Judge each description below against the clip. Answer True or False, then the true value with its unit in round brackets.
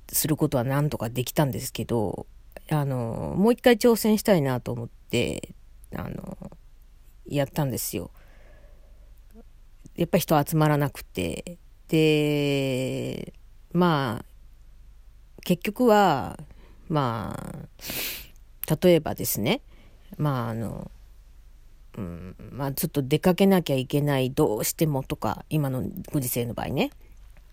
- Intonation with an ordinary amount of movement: False (6.1 semitones)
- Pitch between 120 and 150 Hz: True (140 Hz)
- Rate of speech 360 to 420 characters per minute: False (230 characters per minute)